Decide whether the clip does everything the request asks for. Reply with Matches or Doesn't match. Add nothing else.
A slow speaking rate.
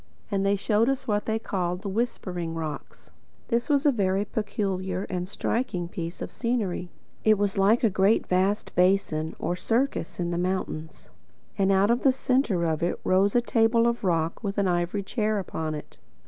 Doesn't match